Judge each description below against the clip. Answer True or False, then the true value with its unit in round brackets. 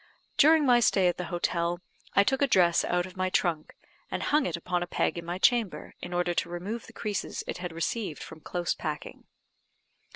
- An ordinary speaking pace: False (215 wpm)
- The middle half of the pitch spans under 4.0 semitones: True (3.6 semitones)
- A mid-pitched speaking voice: True (180 Hz)